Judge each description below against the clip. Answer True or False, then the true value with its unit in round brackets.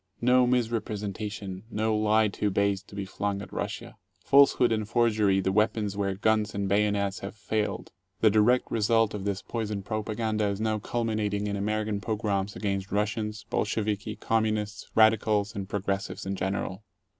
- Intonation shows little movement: True (1.5 semitones)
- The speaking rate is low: False (155 wpm)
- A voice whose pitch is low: True (105 Hz)